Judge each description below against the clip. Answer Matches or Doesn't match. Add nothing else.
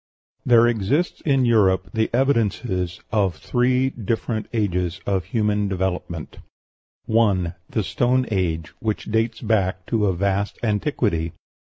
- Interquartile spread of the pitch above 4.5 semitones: Doesn't match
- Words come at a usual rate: Doesn't match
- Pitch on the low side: Matches